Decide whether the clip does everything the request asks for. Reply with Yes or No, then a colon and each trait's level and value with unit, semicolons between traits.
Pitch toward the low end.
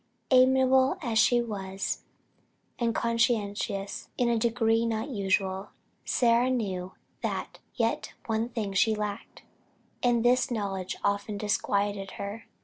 No: high, 220 Hz